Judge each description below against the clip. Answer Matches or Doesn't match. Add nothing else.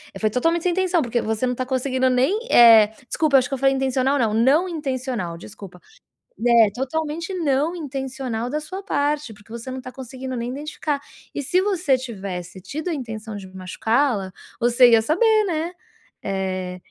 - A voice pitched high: Matches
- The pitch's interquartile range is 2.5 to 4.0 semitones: Doesn't match